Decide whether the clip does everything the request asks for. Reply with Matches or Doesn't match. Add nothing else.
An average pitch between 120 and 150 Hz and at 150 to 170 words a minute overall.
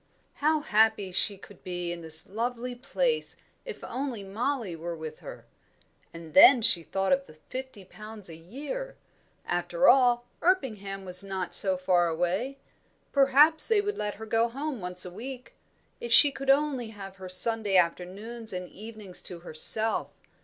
Doesn't match